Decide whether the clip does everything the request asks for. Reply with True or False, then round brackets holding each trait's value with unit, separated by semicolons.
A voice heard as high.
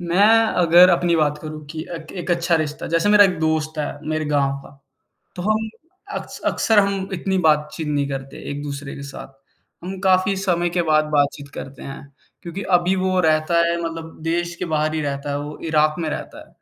False (160 Hz)